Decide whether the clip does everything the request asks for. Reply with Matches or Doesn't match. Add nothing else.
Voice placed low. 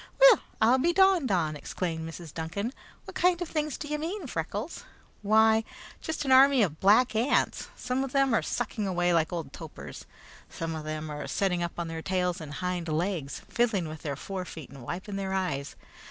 Doesn't match